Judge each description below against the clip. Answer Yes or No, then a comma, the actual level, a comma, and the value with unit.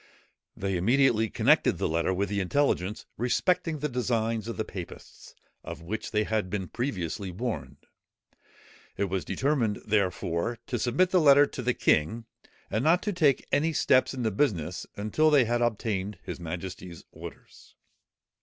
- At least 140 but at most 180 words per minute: Yes, average, 155 wpm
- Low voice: Yes, low, 110 Hz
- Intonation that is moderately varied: No, wide, 6.0 semitones